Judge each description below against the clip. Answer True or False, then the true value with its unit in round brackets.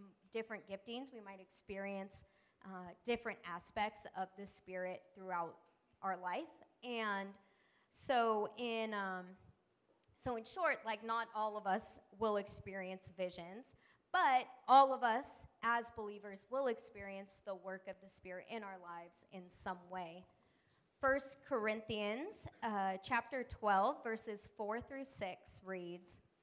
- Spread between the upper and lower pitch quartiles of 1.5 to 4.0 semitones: True (3.5 semitones)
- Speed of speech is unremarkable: False (130 wpm)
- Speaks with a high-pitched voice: True (205 Hz)